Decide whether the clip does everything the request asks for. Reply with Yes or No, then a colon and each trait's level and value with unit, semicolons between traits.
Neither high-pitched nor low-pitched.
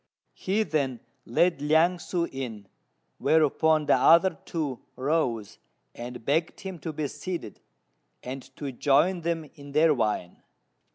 Yes: medium, 150 Hz